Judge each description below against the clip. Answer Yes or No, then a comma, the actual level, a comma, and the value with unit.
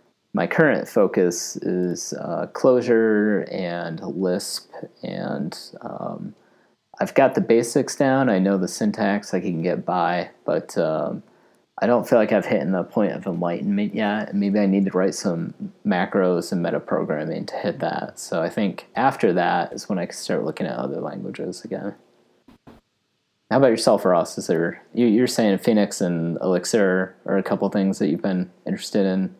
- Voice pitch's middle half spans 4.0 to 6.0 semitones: Yes, average, 5.3 semitones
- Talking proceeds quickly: No, average, 175 wpm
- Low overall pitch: Yes, low, 100 Hz